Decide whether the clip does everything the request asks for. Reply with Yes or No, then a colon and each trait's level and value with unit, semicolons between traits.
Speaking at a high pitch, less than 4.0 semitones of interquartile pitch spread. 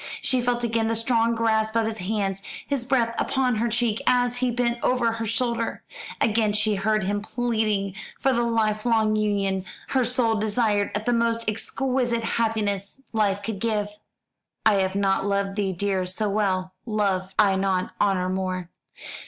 Yes: high, 220 Hz; average, 2.7 semitones